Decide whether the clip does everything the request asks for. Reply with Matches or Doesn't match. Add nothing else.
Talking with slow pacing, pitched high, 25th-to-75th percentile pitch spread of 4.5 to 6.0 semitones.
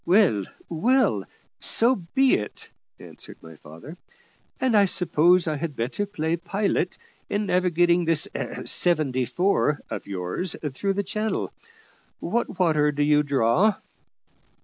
Doesn't match